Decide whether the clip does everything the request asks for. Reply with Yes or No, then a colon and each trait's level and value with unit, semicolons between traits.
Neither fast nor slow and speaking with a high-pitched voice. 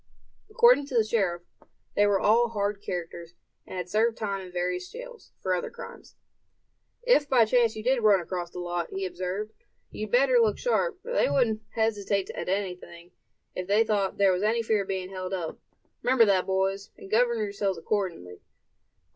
Yes: average, 180 wpm; high, 200 Hz